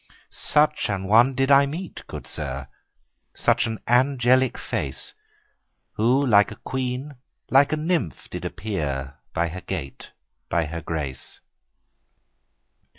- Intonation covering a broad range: Yes, wide, 8.6 semitones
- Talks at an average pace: No, slow, 130 wpm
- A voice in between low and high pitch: No, low, 110 Hz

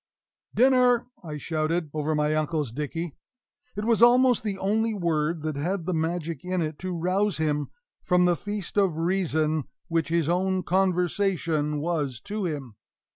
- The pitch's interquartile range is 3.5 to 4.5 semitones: Yes, average, 3.8 semitones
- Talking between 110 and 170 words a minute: Yes, average, 155 wpm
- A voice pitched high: No, medium, 170 Hz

